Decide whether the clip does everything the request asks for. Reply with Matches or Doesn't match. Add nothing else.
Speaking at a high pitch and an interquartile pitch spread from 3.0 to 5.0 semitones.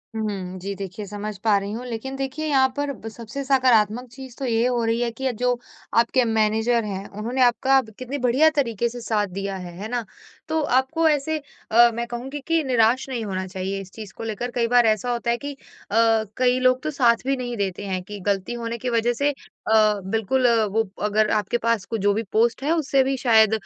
Matches